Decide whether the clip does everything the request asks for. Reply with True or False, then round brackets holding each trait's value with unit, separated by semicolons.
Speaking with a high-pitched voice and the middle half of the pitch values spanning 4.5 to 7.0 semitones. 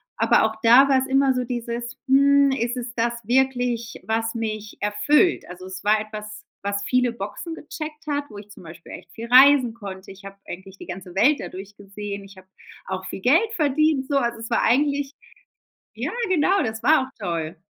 True (235 Hz; 5.0 semitones)